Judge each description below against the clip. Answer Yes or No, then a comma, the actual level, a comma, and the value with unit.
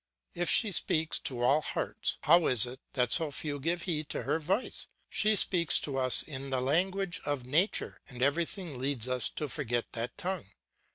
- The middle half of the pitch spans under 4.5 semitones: No, average, 5.0 semitones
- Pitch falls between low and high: Yes, medium, 145 Hz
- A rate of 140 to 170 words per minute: No, average, 185 wpm